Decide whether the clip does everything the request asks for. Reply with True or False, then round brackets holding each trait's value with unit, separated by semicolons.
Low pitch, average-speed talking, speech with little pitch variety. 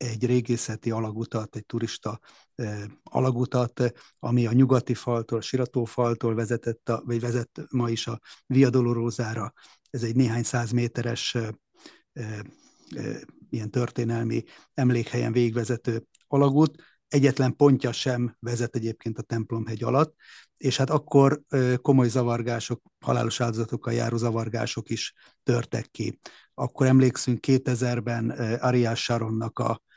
True (120 Hz; 125 wpm; 1.5 semitones)